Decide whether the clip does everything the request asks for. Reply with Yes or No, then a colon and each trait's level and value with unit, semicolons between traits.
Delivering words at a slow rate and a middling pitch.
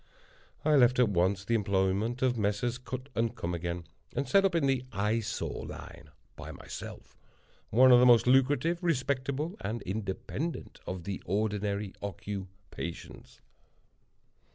No: slow, 130 wpm; low, 115 Hz